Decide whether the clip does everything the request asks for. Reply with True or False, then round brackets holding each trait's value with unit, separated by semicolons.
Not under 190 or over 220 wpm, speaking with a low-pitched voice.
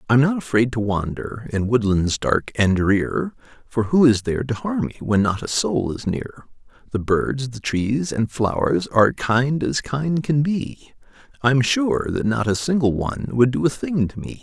True (200 wpm; 125 Hz)